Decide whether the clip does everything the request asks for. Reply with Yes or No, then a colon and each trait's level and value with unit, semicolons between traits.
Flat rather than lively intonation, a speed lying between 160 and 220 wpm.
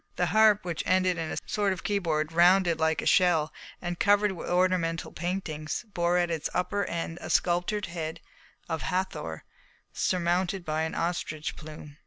Yes: narrow, 2.3 semitones; average, 165 wpm